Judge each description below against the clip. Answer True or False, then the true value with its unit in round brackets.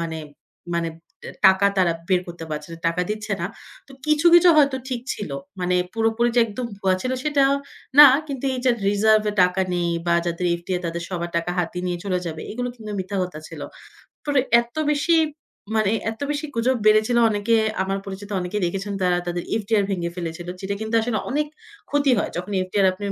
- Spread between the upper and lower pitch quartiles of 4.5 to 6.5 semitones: True (4.9 semitones)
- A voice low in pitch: False (200 Hz)